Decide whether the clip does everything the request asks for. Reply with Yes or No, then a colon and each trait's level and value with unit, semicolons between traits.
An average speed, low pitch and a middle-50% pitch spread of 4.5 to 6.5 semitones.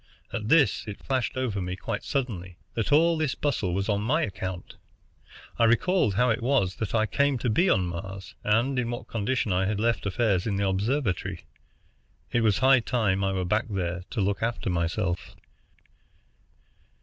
Yes: average, 180 wpm; low, 110 Hz; average, 4.8 semitones